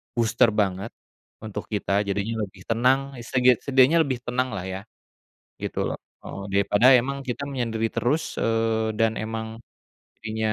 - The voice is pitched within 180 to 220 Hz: No, low, 115 Hz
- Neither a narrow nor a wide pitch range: Yes, average, 3.0 semitones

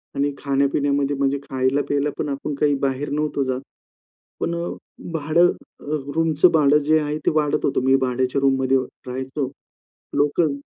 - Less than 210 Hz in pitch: Yes, medium, 140 Hz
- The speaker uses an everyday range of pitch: No, narrow, 2.0 semitones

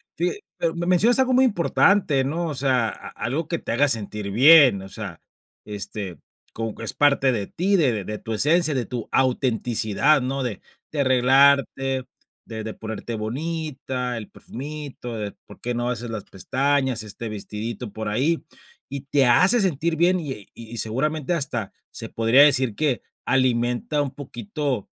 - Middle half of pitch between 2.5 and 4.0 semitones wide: No, average, 4.9 semitones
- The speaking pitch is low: Yes, low, 130 Hz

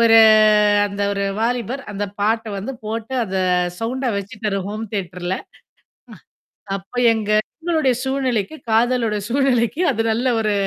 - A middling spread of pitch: Yes, average, 3.5 semitones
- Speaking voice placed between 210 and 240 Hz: Yes, high, 225 Hz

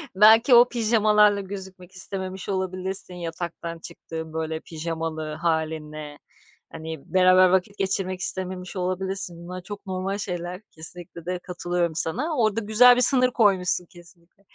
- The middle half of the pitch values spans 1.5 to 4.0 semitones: Yes, average, 2.9 semitones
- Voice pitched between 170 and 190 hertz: Yes, medium, 185 Hz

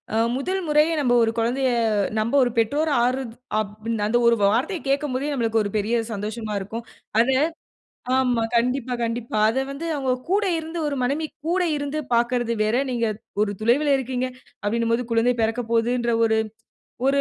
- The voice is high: Yes, high, 245 Hz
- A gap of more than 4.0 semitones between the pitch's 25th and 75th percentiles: No, average, 3.3 semitones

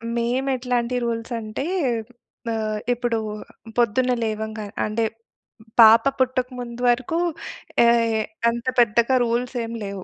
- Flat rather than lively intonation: Yes, narrow, 1.7 semitones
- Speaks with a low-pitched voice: No, high, 235 Hz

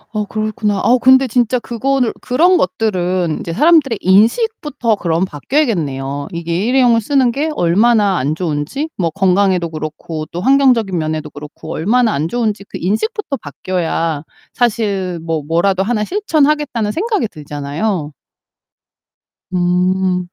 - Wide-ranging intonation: Yes, wide, 6.7 semitones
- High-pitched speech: Yes, high, 200 Hz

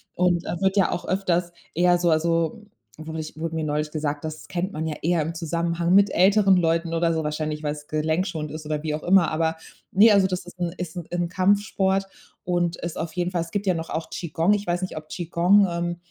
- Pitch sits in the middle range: Yes, medium, 170 Hz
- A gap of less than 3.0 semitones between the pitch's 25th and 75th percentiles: Yes, narrow, 2.4 semitones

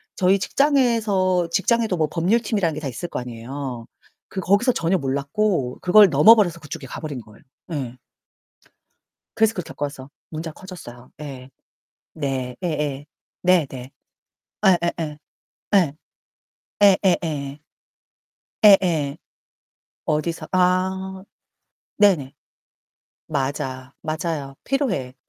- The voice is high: No, medium, 165 Hz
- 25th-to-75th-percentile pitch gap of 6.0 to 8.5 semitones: No, wide, 5.6 semitones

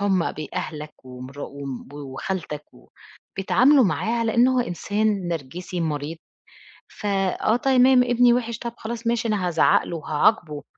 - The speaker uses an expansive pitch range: Yes, wide, 7.3 semitones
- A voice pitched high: Yes, high, 195 Hz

